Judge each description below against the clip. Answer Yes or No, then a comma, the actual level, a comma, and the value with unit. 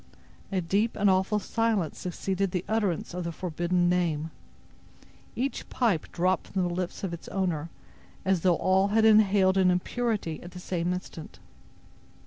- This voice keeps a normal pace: Yes, average, 155 wpm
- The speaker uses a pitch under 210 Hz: Yes, medium, 185 Hz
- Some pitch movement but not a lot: No, narrow, 2.3 semitones